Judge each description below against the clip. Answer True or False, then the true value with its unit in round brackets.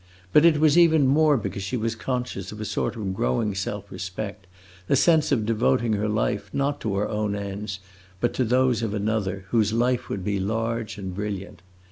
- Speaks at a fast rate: False (195 wpm)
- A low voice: True (110 Hz)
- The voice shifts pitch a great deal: False (3.8 semitones)